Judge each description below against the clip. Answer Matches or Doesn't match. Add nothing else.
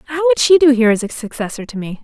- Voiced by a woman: Matches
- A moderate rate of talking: Doesn't match